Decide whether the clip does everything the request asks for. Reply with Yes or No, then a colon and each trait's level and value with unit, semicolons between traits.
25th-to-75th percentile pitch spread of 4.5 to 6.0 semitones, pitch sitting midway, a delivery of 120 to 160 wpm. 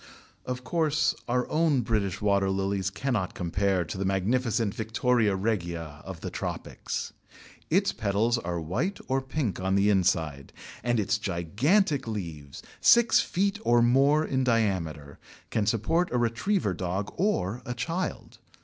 No: wide, 5.6 semitones; low, 110 Hz; average, 140 wpm